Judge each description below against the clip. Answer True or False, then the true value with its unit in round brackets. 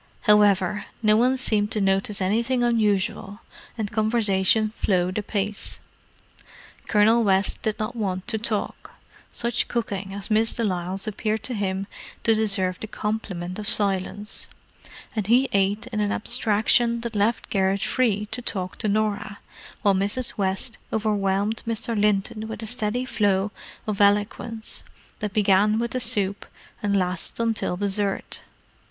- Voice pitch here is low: False (210 Hz)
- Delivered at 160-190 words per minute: False (145 wpm)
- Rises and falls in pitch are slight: True (2.2 semitones)